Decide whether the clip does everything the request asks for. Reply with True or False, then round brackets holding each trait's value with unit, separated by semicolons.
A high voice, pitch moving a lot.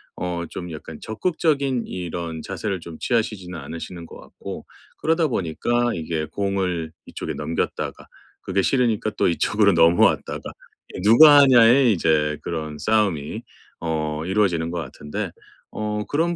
False (95 Hz; 5.7 semitones)